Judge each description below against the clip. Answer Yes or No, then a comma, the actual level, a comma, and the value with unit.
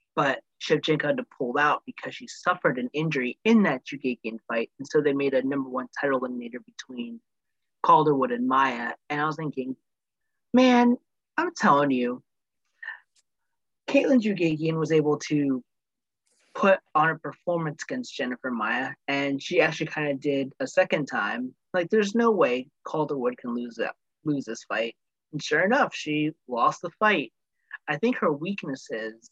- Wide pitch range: Yes, wide, 6.8 semitones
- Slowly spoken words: No, average, 160 wpm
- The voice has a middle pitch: Yes, medium, 150 Hz